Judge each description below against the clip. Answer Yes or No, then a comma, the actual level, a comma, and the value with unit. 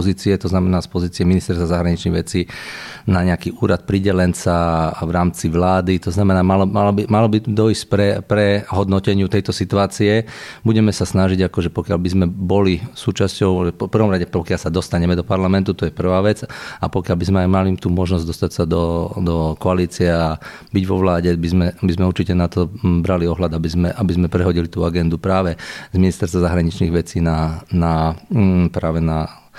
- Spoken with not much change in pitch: Yes, narrow, 2.2 semitones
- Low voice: Yes, very low, 90 Hz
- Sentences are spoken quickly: Yes, fast, 185 wpm